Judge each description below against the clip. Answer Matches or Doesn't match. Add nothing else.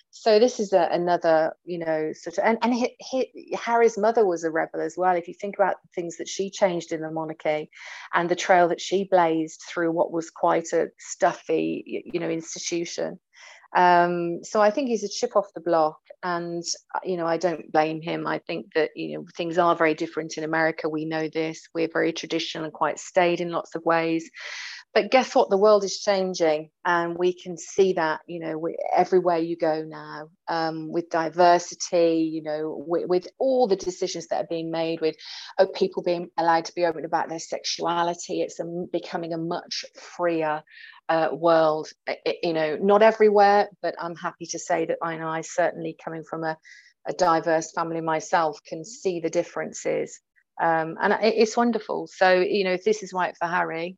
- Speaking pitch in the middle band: Matches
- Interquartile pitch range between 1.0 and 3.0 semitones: Matches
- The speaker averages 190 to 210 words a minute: Matches